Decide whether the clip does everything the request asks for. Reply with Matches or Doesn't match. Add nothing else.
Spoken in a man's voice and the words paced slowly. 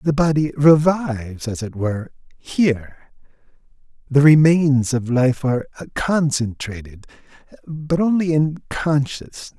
Matches